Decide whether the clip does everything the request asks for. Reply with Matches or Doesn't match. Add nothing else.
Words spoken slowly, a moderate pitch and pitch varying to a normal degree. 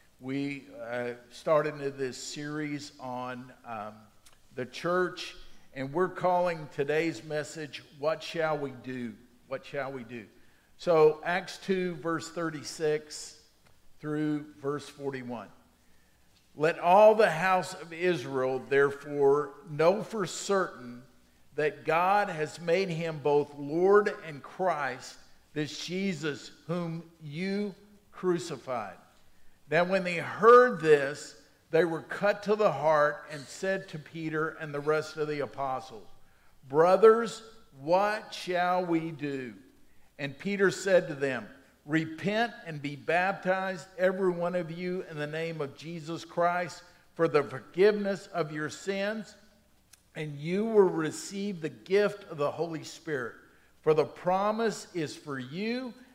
Matches